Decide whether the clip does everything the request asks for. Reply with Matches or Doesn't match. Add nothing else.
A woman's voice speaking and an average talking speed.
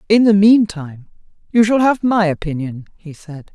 Matches